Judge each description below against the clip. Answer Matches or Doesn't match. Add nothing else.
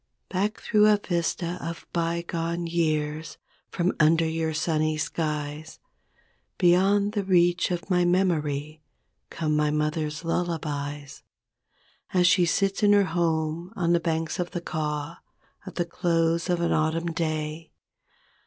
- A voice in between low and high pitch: Matches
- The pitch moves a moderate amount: Doesn't match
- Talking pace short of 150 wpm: Matches